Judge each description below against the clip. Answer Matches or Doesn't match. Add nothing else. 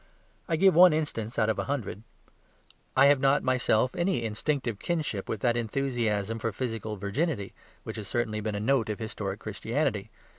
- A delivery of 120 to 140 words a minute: Doesn't match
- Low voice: Matches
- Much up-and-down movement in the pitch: Doesn't match